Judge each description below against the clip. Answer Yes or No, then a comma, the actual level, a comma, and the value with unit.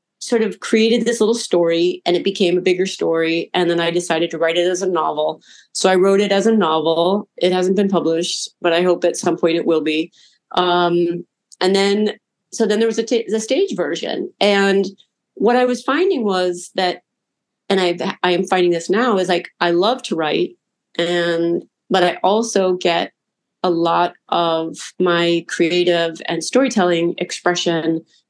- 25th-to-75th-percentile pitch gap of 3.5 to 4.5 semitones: No, average, 2.9 semitones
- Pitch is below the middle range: No, medium, 180 Hz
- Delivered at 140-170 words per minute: No, average, 185 wpm